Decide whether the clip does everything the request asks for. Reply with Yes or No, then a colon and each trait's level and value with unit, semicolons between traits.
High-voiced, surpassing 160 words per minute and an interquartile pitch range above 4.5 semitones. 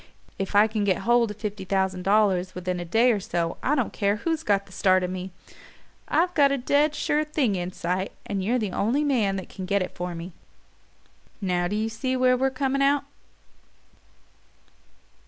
Yes: high, 205 Hz; average, 195 wpm; wide, 5.5 semitones